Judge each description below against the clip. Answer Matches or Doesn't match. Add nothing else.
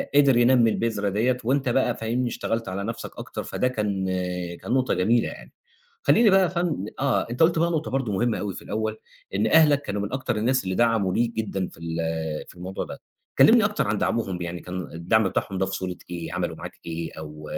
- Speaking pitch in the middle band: Doesn't match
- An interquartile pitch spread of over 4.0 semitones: Matches